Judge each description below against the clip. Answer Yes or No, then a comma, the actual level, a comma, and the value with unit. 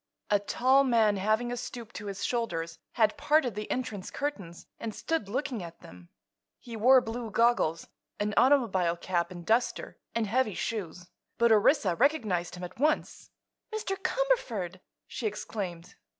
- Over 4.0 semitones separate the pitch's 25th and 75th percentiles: Yes, average, 5.3 semitones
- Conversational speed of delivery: Yes, average, 150 wpm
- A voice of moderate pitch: No, high, 220 Hz